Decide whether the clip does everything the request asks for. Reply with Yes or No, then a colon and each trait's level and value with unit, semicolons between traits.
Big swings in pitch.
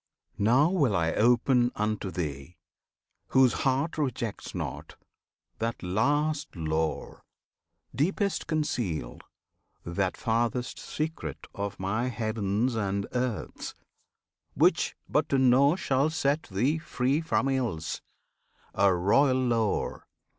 Yes: wide, 5.9 semitones